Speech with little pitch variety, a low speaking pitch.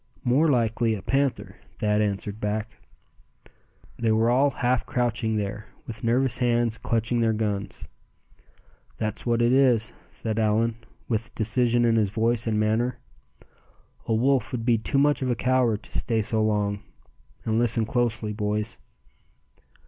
Yes: narrow, 2.1 semitones; low, 115 Hz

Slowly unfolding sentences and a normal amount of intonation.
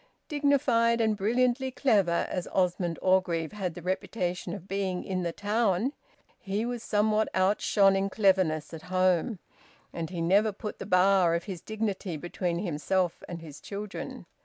No: average, 155 wpm; average, 3.4 semitones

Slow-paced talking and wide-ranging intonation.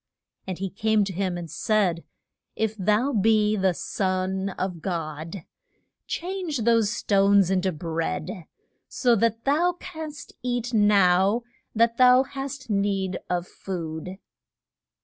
No: slow, 130 wpm; average, 3.9 semitones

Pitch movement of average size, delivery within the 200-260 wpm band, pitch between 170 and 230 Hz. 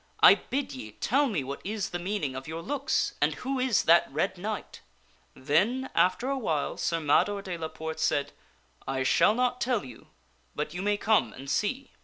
No: wide, 8.3 semitones; fast, 205 wpm; medium, 185 Hz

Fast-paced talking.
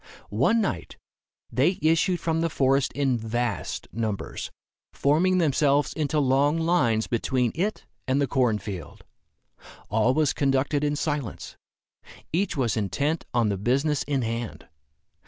No: slow, 135 wpm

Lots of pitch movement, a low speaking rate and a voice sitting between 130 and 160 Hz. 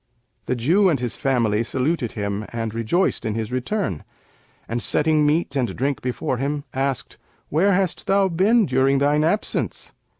No: wide, 5.7 semitones; average, 160 wpm; low, 135 Hz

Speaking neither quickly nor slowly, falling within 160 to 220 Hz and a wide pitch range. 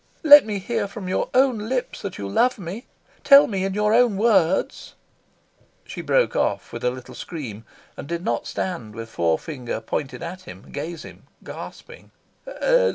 Yes: average, 165 wpm; medium, 185 Hz; wide, 8.2 semitones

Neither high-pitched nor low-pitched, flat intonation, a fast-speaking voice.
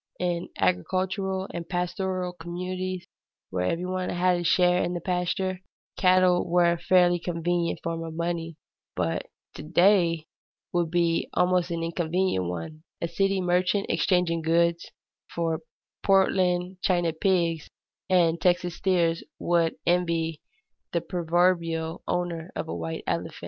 No: medium, 175 Hz; narrow, 1.6 semitones; slow, 135 wpm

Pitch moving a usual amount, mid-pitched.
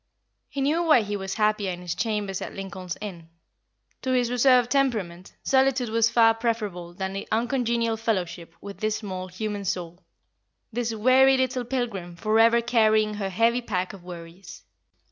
No: average, 4.2 semitones; high, 215 Hz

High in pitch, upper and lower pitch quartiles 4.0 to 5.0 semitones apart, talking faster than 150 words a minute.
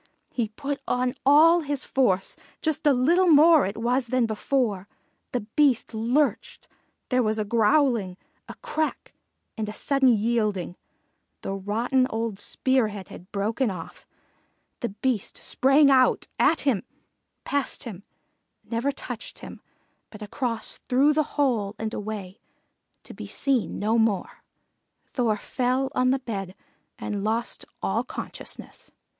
No: high, 240 Hz; average, 4.3 semitones; average, 140 wpm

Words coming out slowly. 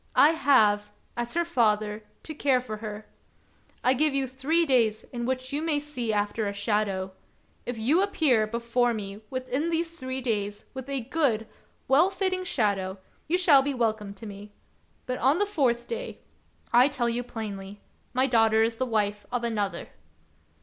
No: average, 175 wpm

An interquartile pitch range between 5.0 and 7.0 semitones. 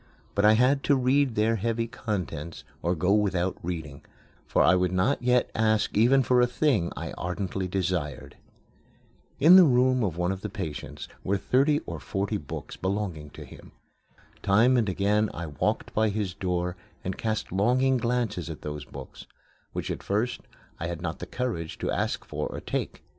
Yes: wide, 5.4 semitones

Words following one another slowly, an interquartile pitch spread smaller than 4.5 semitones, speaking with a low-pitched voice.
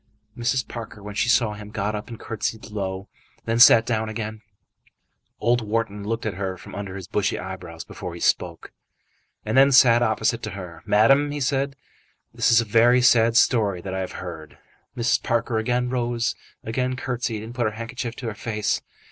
No: average, 190 wpm; average, 2.7 semitones; low, 110 Hz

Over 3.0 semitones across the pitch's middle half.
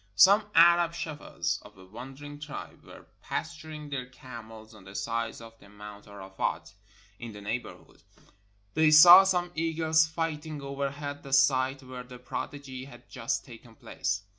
Yes: wide, 5.5 semitones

